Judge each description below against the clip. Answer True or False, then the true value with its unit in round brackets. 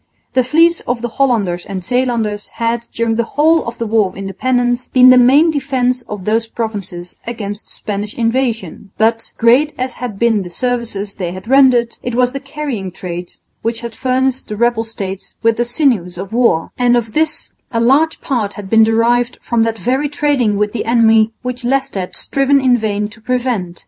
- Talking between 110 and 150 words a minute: False (190 wpm)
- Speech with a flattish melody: False (3.3 semitones)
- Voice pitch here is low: False (235 Hz)